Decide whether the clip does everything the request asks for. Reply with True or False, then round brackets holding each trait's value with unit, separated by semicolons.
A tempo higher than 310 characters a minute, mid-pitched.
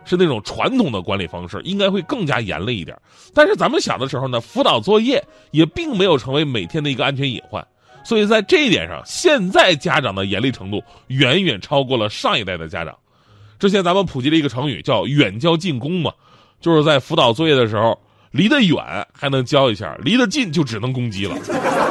True (325 characters per minute; 145 Hz)